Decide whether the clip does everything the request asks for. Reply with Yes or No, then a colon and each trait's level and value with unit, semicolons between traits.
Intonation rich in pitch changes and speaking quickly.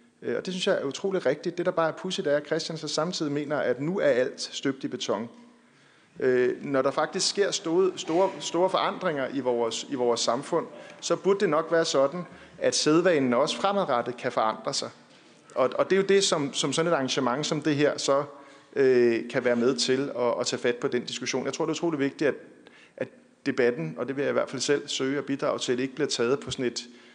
Yes: wide, 5.8 semitones; fast, 235 wpm